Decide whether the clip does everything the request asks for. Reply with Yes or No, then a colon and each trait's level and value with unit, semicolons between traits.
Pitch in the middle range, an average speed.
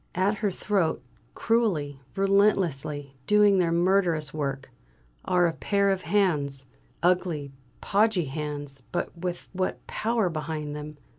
No: medium, 175 Hz; slow, 125 wpm